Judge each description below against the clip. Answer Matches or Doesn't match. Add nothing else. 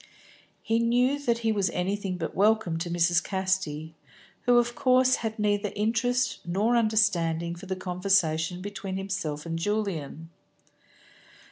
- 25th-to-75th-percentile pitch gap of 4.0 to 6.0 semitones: Matches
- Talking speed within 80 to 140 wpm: Matches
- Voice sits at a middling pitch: Doesn't match